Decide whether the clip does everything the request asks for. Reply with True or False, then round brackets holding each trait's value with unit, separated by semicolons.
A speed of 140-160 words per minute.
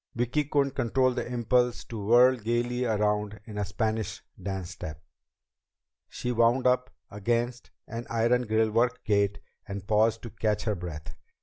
True (145 wpm)